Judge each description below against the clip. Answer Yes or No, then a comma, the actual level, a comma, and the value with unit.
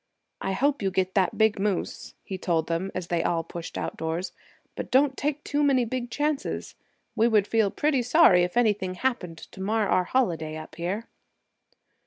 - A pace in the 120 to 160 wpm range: No, average, 175 wpm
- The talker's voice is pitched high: Yes, high, 200 Hz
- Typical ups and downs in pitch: No, wide, 6.0 semitones